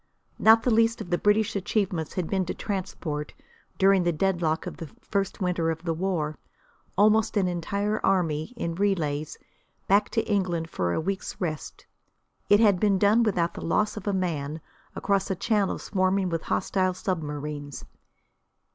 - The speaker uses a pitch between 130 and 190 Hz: Yes, medium, 185 Hz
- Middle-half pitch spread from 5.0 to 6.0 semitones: No, average, 3.8 semitones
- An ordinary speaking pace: Yes, average, 165 wpm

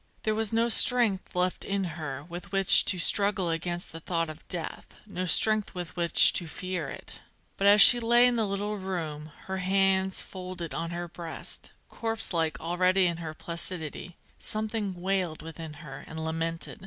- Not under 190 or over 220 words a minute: No, average, 175 wpm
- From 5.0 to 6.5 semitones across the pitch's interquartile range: No, average, 3.2 semitones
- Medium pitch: Yes, medium, 180 Hz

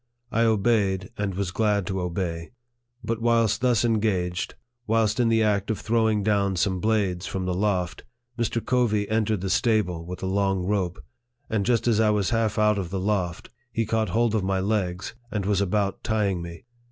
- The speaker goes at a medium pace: Yes, average, 190 wpm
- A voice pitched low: Yes, low, 105 Hz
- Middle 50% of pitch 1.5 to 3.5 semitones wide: Yes, average, 2.9 semitones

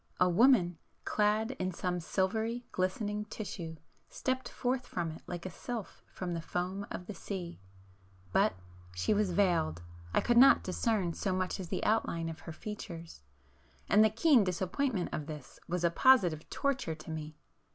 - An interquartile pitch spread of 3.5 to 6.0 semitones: Yes, average, 4.7 semitones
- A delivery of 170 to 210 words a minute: No, average, 155 wpm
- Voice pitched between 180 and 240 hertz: Yes, medium, 185 Hz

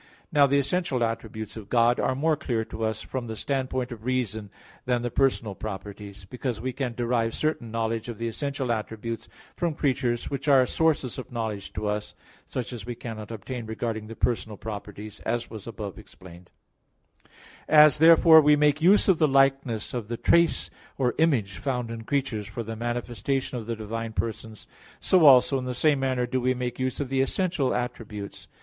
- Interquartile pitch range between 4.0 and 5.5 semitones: No, average, 3.5 semitones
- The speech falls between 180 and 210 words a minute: Yes, average, 195 wpm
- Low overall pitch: Yes, low, 120 Hz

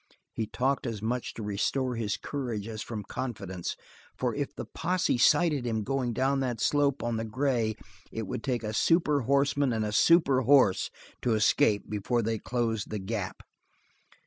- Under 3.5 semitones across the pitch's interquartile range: No, average, 4.0 semitones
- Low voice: Yes, low, 120 Hz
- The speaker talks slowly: No, average, 175 wpm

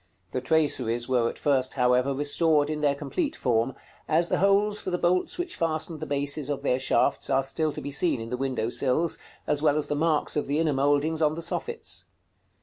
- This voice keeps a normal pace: No, fast, 215 wpm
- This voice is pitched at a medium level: Yes, medium, 145 Hz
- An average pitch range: Yes, average, 3.4 semitones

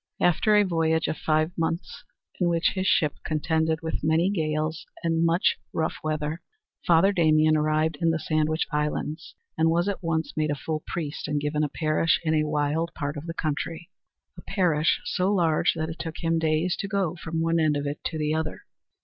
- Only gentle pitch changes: Yes, narrow, 1.4 semitones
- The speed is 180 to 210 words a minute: Yes, average, 200 wpm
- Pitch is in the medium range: Yes, medium, 160 Hz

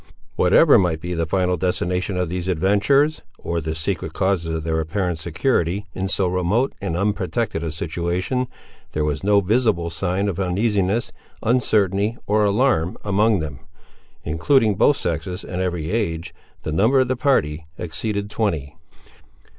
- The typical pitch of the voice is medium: No, very low, 95 Hz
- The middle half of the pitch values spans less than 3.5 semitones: No, average, 4.1 semitones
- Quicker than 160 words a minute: No, average, 150 wpm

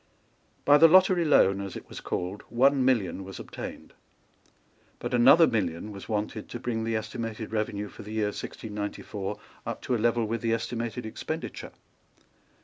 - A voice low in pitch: Yes, low, 110 Hz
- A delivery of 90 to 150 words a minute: No, average, 160 wpm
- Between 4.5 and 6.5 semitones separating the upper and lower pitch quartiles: No, average, 2.9 semitones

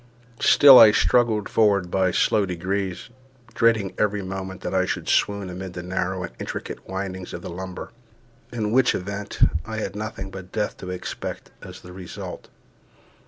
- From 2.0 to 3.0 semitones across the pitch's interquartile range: Yes, narrow, 2.5 semitones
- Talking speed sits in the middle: Yes, average, 165 wpm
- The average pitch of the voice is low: Yes, very low, 95 Hz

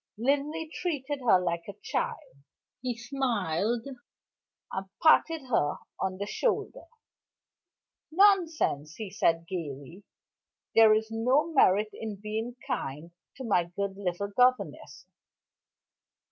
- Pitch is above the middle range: Yes, high, 220 Hz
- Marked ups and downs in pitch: Yes, wide, 6.3 semitones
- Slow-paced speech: Yes, slow, 110 wpm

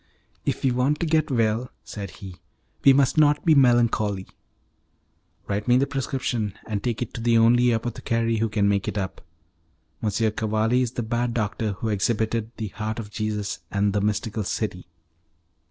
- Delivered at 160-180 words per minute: Yes, average, 170 wpm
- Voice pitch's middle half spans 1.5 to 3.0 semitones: Yes, average, 2.7 semitones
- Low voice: Yes, low, 115 Hz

